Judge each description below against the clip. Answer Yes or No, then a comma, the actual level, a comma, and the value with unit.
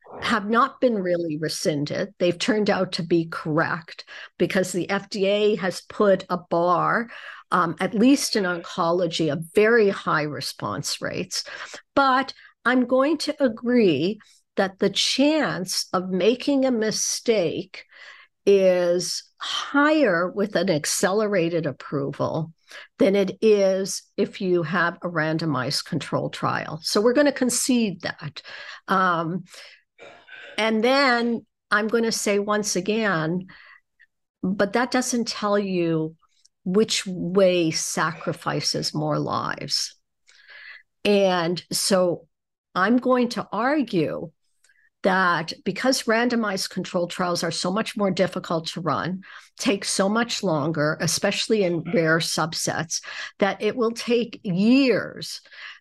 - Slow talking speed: Yes, slow, 120 wpm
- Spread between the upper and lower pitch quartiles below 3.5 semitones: No, average, 4.9 semitones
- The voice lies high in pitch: Yes, high, 195 Hz